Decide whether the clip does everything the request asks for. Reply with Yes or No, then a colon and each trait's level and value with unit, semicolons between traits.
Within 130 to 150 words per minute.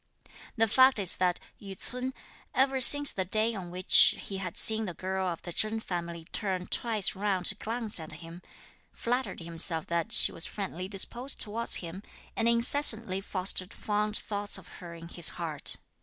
No: average, 175 wpm